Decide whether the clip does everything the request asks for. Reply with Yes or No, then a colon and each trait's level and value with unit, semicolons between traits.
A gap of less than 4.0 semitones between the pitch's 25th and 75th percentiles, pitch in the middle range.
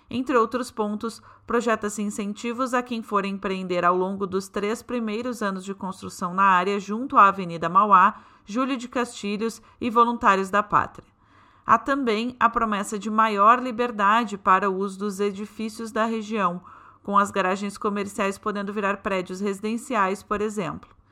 No: narrow, 2.5 semitones; high, 210 Hz